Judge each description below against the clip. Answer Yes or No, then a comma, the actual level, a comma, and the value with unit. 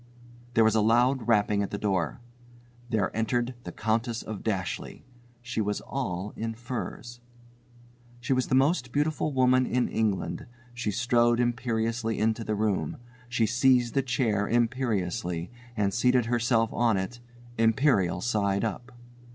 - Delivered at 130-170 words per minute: Yes, average, 145 wpm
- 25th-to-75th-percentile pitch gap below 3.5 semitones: Yes, narrow, 2.6 semitones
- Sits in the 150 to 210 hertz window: No, low, 115 Hz